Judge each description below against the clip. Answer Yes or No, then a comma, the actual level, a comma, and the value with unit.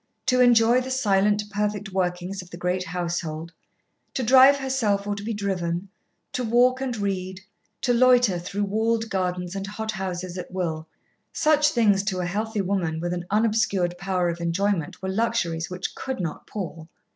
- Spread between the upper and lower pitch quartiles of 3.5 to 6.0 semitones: Yes, average, 4.0 semitones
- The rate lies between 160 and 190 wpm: Yes, average, 165 wpm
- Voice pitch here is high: Yes, high, 195 Hz